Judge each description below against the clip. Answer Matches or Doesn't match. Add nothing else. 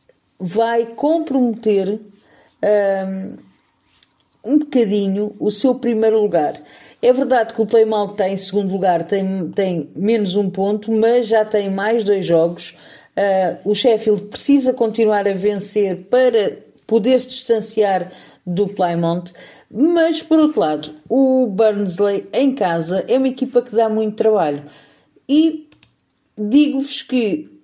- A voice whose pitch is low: Doesn't match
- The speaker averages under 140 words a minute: Matches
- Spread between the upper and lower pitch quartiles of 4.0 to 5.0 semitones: Matches